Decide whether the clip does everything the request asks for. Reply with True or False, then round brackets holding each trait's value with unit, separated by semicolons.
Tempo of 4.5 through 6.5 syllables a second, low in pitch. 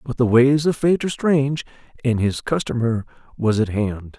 True (5.0 syllables/s; 125 Hz)